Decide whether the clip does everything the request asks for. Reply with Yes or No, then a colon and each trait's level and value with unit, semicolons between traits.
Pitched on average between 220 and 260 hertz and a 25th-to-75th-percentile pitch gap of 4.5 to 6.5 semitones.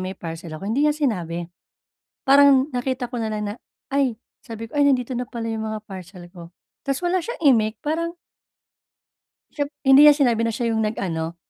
Yes: high, 235 Hz; wide, 5.6 semitones